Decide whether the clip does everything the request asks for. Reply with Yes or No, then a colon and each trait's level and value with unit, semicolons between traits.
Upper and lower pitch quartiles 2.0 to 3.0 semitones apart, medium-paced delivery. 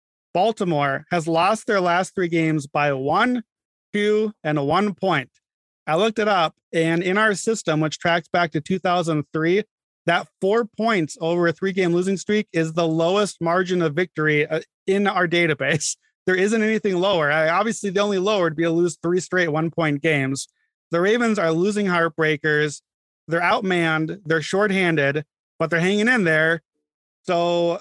No: average, 3.8 semitones; average, 165 wpm